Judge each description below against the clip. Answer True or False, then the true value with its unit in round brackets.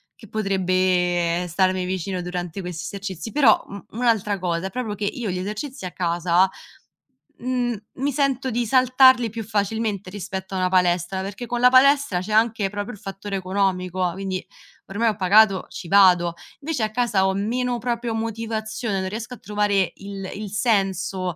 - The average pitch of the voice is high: True (200 Hz)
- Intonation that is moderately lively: True (3.6 semitones)